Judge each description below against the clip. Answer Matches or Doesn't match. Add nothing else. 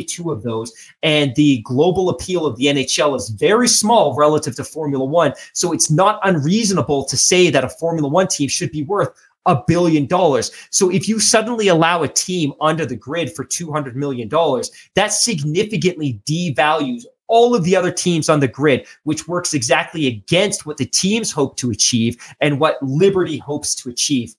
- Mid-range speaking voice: Matches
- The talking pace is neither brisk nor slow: Matches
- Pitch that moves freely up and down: Doesn't match